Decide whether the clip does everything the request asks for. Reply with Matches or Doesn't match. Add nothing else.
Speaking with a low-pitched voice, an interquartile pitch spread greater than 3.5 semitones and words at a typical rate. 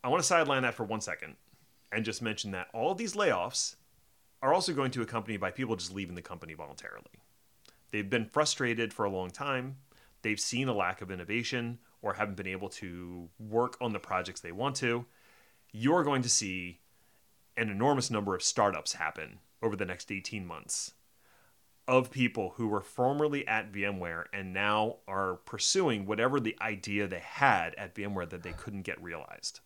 Matches